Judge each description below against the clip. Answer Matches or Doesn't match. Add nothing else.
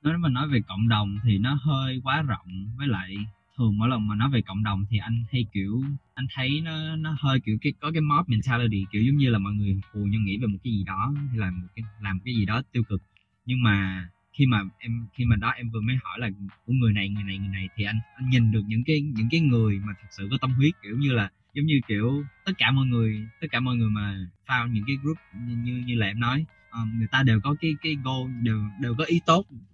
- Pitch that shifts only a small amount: Doesn't match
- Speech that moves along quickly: Matches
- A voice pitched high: Doesn't match